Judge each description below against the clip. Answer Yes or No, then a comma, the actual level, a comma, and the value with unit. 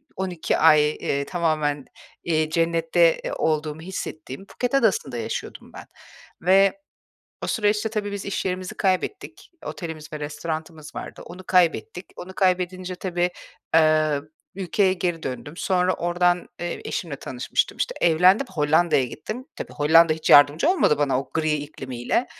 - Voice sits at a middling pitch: Yes, medium, 170 Hz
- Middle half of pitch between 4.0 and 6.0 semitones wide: No, average, 3.5 semitones